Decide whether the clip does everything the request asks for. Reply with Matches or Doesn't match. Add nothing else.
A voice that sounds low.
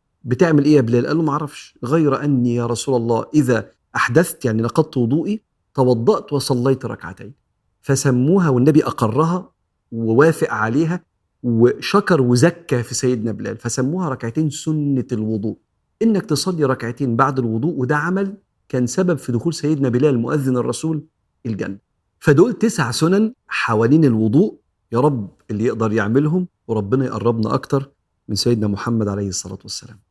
Matches